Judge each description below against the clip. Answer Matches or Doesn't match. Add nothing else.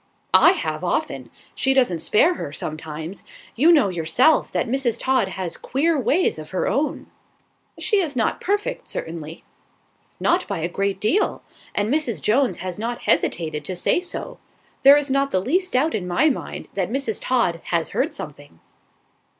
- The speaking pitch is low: Doesn't match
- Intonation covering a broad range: Matches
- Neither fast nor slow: Matches